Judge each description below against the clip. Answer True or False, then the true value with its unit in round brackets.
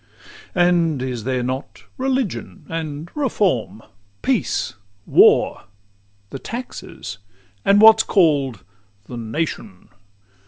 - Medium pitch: True (155 Hz)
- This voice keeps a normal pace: False (95 wpm)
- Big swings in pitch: True (7.9 semitones)